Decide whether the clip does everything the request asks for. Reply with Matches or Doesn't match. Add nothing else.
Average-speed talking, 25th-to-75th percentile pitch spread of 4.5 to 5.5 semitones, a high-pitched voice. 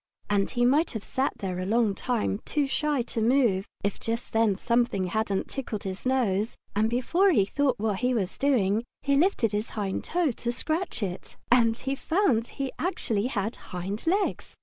Matches